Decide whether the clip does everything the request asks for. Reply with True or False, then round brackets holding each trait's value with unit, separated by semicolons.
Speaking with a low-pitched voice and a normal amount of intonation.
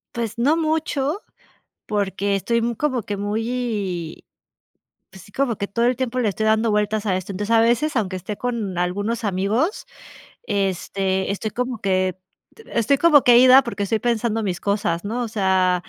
False (215 Hz; 3.7 semitones)